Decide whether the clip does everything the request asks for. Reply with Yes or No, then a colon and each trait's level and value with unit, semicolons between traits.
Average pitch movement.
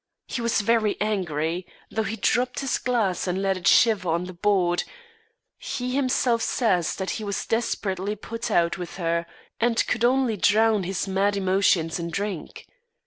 Yes: average, 4.1 semitones